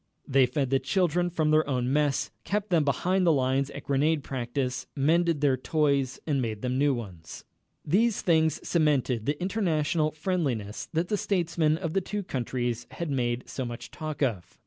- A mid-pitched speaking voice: Yes, medium, 145 Hz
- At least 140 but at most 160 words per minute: No, average, 175 wpm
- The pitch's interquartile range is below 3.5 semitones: No, average, 4.5 semitones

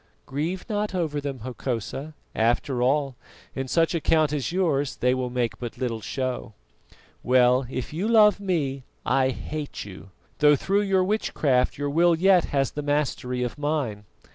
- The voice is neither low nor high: Yes, medium, 145 Hz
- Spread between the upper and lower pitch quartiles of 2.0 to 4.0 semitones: No, average, 4.6 semitones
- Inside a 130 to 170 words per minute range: Yes, average, 165 wpm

